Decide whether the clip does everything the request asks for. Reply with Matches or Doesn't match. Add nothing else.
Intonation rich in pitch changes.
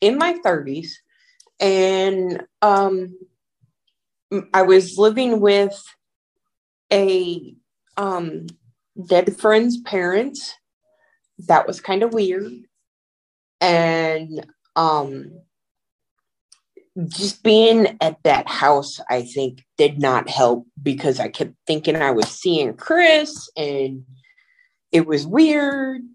Matches